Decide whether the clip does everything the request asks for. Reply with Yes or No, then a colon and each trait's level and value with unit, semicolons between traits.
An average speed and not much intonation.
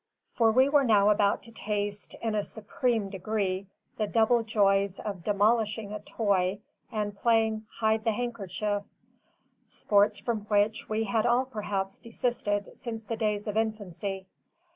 Yes: average, 145 wpm; narrow, 1.7 semitones